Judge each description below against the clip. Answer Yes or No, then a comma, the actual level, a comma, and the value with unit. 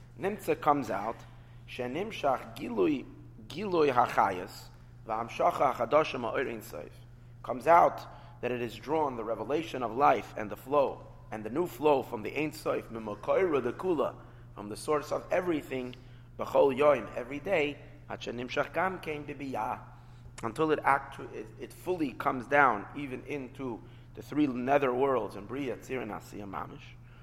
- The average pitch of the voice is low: Yes, low, 125 Hz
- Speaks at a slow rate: Yes, slow, 130 wpm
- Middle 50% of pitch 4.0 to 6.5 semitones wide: No, average, 3.3 semitones